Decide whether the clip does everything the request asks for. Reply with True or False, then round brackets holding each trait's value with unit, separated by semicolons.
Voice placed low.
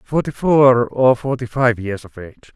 True (125 Hz)